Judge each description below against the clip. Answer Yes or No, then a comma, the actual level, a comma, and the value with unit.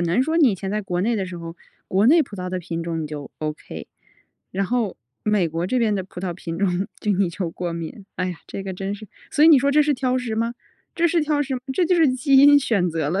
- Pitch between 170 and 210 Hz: Yes, high, 200 Hz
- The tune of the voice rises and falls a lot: Yes, wide, 6.5 semitones